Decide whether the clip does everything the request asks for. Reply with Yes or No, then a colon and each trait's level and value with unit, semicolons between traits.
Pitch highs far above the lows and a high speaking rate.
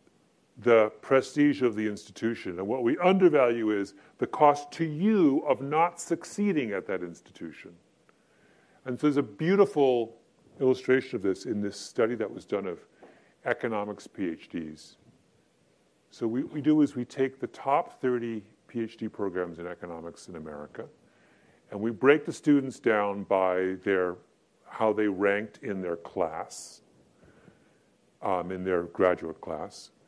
No: wide, 6.4 semitones; average, 145 wpm